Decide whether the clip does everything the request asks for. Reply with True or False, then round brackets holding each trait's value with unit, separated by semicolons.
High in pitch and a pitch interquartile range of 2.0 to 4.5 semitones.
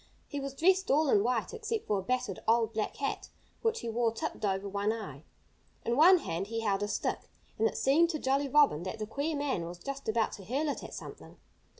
False (235 Hz; 5.6 semitones)